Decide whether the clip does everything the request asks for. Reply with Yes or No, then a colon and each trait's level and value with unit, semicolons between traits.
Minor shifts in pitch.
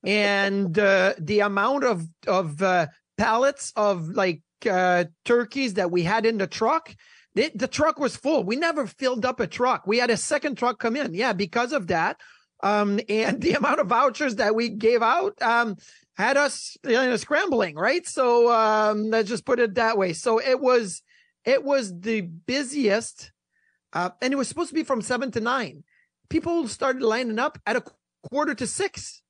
No: average, 4.7 semitones